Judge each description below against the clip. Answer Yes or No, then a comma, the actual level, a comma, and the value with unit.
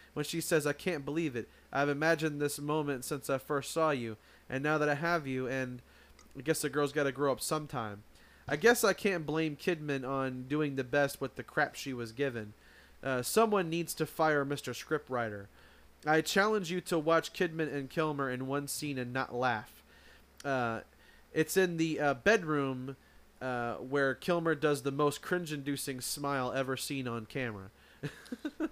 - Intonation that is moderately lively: Yes, average, 3.4 semitones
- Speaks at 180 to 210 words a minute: Yes, average, 185 wpm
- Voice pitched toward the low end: No, medium, 145 Hz